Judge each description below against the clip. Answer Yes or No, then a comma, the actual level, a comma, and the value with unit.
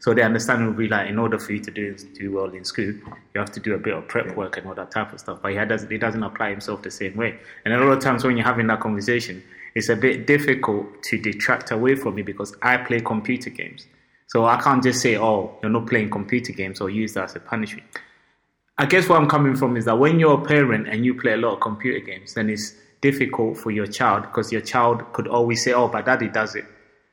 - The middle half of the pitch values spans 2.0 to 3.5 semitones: Yes, average, 2.9 semitones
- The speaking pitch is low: Yes, low, 115 Hz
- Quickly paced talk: Yes, fast, 265 wpm